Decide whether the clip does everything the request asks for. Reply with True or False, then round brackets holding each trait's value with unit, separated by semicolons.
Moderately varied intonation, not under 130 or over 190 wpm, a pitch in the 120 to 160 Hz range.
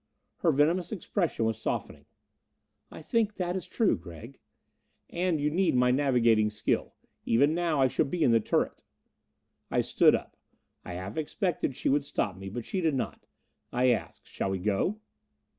False (7.6 semitones; 170 wpm; 140 Hz)